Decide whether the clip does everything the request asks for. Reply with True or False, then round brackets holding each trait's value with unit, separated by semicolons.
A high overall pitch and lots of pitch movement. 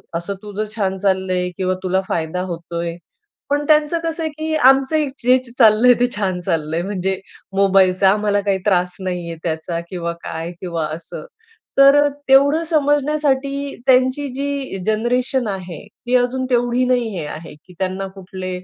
True (205 Hz; 6.6 semitones)